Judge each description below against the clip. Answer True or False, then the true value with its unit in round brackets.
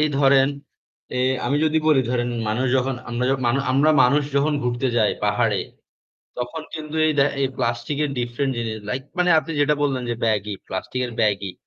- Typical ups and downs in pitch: True (3.4 semitones)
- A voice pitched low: True (130 Hz)